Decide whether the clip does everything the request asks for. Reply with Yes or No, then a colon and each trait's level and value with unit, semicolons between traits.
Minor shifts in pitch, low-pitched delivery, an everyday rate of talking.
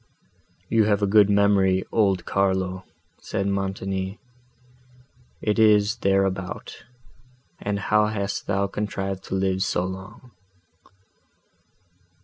No: narrow, 1.4 semitones; low, 100 Hz; slow, 105 wpm